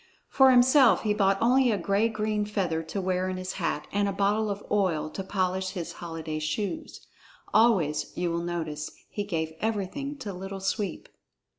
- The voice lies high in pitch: Yes, high, 195 Hz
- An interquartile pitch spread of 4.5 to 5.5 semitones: No, average, 3.7 semitones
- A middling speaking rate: Yes, average, 175 wpm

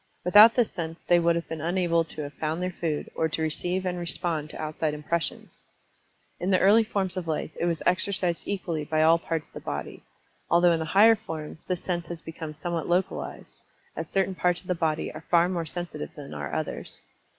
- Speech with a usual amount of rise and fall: No, narrow, 2.3 semitones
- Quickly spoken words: Yes, fast, 210 wpm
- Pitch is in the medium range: Yes, medium, 170 Hz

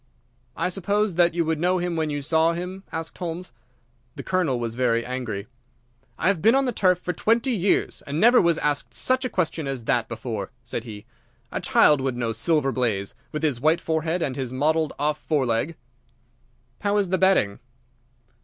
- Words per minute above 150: Yes, average, 190 wpm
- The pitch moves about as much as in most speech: No, wide, 6.1 semitones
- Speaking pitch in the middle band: Yes, medium, 160 Hz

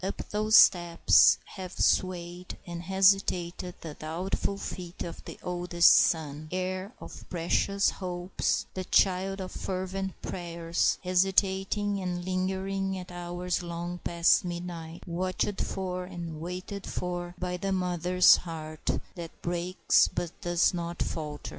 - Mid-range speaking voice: Yes, medium, 180 Hz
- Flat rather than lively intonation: Yes, narrow, 1.6 semitones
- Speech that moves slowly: Yes, slow, 130 wpm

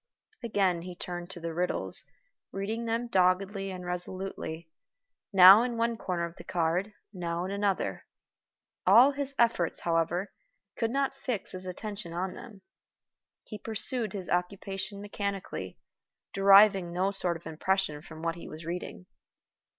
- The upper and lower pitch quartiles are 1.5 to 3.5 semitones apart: Yes, average, 3.1 semitones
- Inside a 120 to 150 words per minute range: Yes, average, 145 wpm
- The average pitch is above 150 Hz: Yes, high, 190 Hz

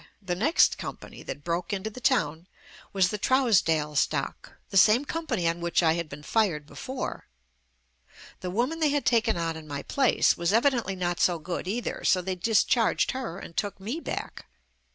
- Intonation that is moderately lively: No, wide, 5.9 semitones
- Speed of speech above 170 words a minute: Yes, average, 190 wpm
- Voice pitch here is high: Yes, high, 195 Hz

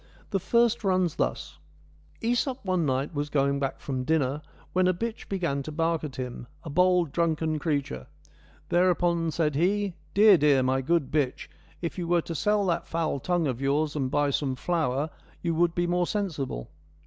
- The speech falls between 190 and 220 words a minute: No, average, 170 wpm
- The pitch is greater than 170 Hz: No, medium, 160 Hz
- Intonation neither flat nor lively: Yes, average, 4.2 semitones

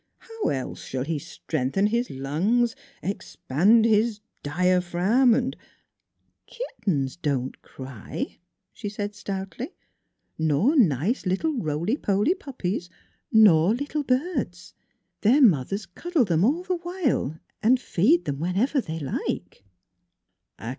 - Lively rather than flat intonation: Yes, wide, 7.9 semitones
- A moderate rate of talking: No, slow, 125 wpm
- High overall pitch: Yes, high, 200 Hz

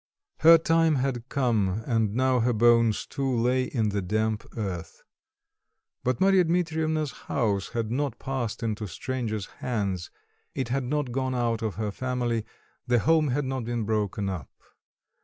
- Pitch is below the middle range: Yes, low, 120 Hz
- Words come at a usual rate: Yes, average, 155 wpm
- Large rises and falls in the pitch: No, average, 3.8 semitones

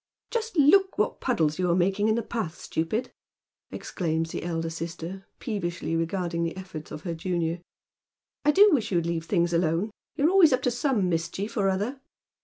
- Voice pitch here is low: No, medium, 185 Hz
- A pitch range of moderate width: No, wide, 6.0 semitones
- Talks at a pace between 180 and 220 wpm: Yes, average, 190 wpm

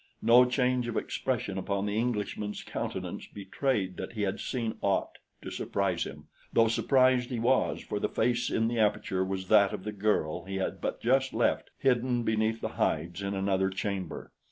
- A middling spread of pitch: Yes, average, 3.9 semitones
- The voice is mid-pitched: No, low, 110 Hz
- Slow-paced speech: No, average, 180 wpm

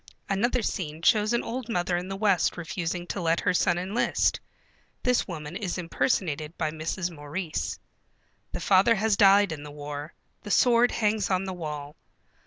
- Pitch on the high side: No, medium, 180 Hz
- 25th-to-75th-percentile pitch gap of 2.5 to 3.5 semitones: No, average, 4.3 semitones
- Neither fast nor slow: Yes, average, 170 wpm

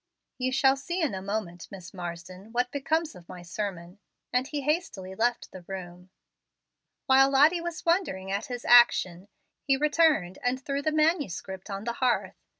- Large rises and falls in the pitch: Yes, wide, 7.2 semitones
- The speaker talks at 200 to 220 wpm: No, average, 165 wpm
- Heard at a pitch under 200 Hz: No, high, 240 Hz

